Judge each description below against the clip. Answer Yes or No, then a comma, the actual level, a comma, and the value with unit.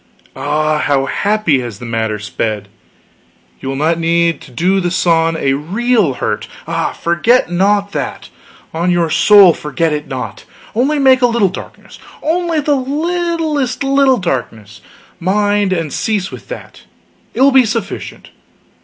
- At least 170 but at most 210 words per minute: No, average, 150 wpm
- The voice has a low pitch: No, medium, 185 Hz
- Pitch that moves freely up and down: Yes, wide, 8.5 semitones